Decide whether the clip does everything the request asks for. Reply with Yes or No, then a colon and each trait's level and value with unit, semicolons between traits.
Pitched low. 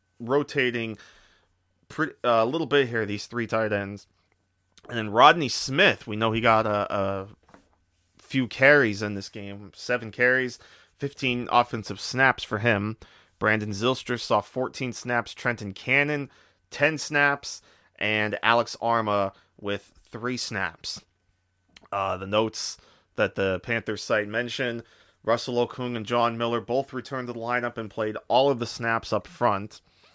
Yes: low, 115 Hz